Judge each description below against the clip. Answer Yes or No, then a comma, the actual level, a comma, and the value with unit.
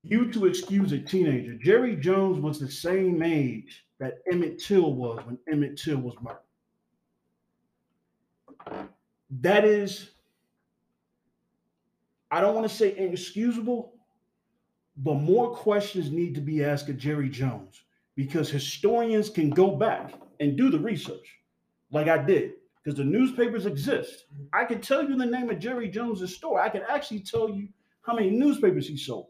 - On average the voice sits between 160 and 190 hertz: Yes, medium, 185 Hz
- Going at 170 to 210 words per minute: No, average, 150 wpm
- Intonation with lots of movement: Yes, wide, 7.2 semitones